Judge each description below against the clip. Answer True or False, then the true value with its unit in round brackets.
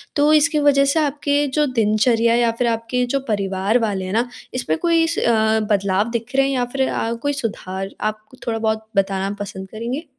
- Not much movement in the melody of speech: False (4.5 semitones)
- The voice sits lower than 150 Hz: False (230 Hz)